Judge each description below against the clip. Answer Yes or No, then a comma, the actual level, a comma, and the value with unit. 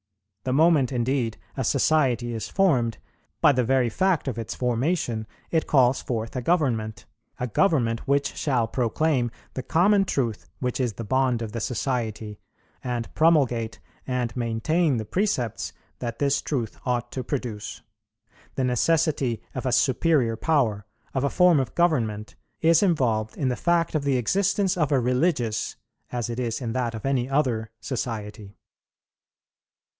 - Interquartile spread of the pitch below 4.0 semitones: No, average, 4.3 semitones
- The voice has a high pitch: No, low, 125 Hz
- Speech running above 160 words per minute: No, average, 155 wpm